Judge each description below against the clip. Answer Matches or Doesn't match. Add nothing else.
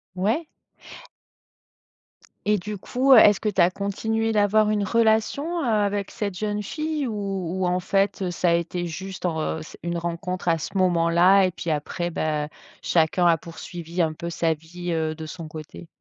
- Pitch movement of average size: Matches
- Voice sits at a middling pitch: Matches